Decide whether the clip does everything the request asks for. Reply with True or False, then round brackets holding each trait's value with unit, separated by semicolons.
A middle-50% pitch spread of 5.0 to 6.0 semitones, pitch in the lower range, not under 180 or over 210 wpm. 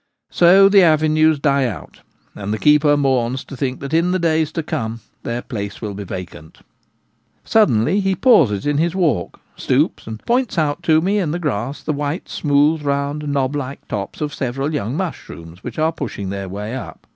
False (5.4 semitones; 145 Hz; 190 wpm)